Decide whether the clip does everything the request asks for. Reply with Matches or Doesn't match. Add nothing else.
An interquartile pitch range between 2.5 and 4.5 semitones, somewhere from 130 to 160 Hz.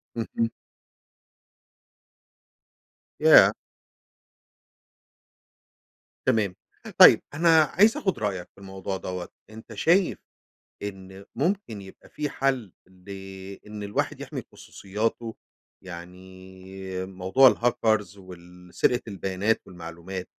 Doesn't match